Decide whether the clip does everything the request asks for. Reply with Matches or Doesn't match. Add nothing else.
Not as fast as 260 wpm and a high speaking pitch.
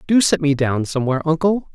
Doesn't match